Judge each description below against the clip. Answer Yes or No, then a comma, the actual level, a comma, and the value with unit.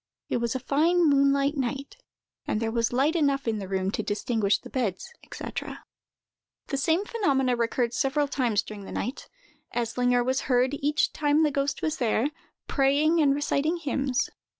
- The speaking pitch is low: No, very high, 270 Hz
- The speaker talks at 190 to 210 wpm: No, average, 170 wpm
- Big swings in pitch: No, average, 3.5 semitones